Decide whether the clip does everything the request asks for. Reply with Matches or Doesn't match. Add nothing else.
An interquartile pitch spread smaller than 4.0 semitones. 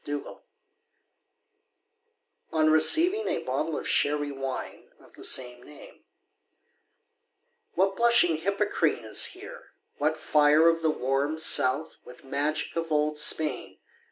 Matches